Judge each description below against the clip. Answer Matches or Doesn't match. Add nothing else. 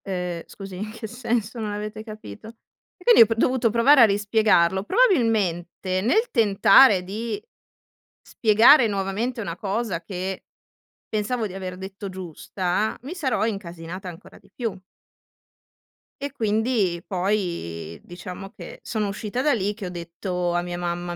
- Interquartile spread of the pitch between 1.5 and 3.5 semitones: Doesn't match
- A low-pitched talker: Doesn't match